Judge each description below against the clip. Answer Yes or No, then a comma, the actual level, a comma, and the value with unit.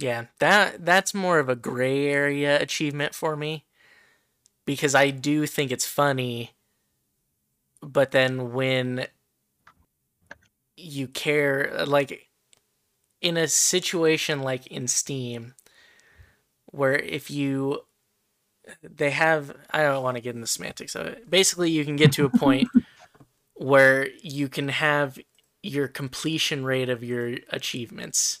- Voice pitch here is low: No, medium, 145 Hz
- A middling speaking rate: No, slow, 130 wpm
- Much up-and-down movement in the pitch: No, average, 2.9 semitones